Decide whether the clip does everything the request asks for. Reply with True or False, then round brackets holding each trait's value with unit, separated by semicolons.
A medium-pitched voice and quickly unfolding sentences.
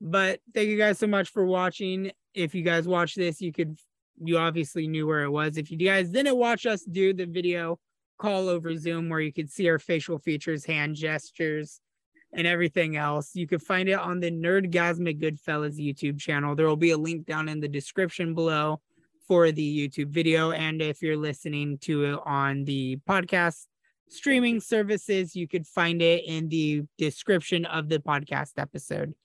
False (165 Hz; 190 wpm)